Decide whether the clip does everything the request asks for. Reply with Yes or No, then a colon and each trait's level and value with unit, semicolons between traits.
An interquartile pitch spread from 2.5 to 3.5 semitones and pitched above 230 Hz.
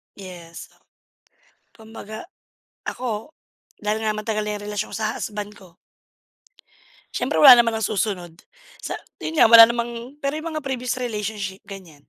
No: average, 2.8 semitones; high, 220 Hz